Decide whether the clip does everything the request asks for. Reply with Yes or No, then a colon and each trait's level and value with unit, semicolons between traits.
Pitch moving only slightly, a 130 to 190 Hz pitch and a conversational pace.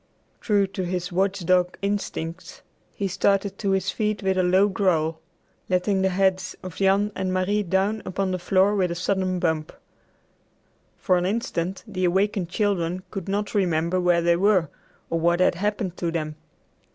Yes: narrow, 2.0 semitones; medium, 185 Hz; average, 165 wpm